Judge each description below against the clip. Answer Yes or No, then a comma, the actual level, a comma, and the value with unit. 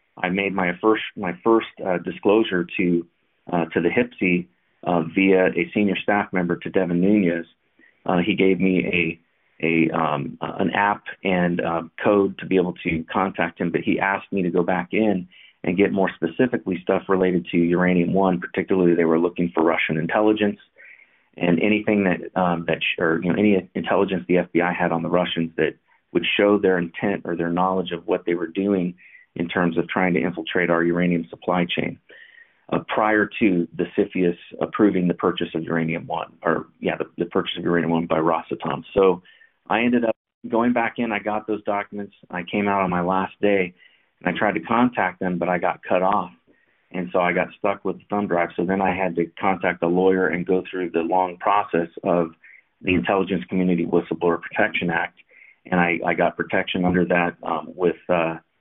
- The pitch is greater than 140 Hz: No, very low, 90 Hz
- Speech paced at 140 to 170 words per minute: No, average, 200 wpm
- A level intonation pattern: Yes, narrow, 2.3 semitones